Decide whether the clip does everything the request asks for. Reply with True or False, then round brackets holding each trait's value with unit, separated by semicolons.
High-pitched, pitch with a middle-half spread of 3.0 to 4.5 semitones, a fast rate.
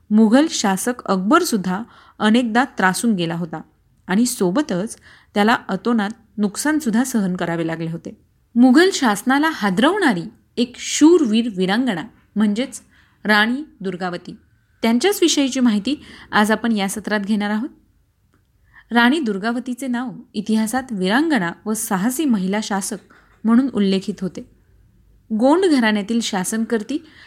False (225 Hz; 4.0 semitones; 110 wpm)